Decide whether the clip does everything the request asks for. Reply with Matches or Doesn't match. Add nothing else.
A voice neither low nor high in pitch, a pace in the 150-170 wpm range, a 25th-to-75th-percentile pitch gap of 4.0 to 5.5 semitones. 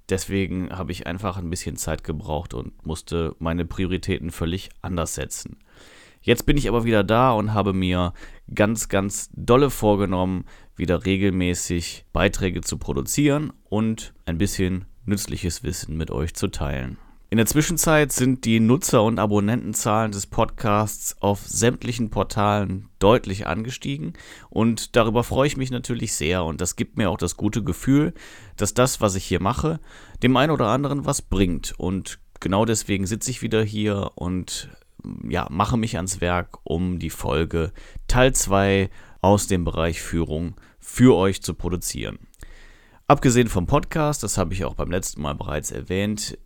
Doesn't match